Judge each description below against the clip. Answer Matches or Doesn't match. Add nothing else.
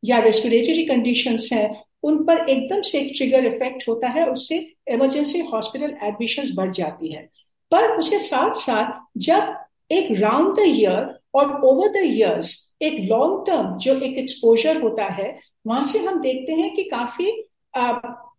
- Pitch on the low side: Doesn't match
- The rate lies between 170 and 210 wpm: Doesn't match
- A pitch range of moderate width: Doesn't match